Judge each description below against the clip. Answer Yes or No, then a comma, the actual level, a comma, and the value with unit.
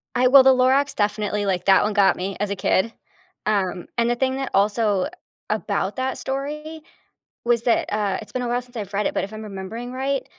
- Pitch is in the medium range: No, high, 225 Hz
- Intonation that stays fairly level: No, average, 4.3 semitones